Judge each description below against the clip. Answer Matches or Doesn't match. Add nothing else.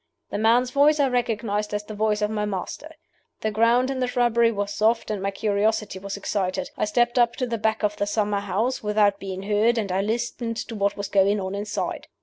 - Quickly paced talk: Matches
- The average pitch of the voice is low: Doesn't match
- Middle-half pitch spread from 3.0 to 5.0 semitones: Doesn't match